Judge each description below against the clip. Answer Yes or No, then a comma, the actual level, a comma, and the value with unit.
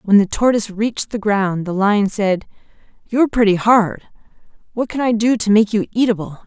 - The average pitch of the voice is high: Yes, high, 210 Hz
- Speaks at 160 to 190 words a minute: Yes, average, 185 wpm